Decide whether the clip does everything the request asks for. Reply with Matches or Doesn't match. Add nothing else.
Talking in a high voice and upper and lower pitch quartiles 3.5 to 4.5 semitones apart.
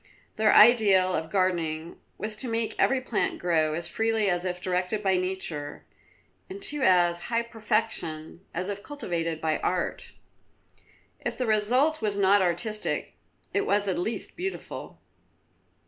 Matches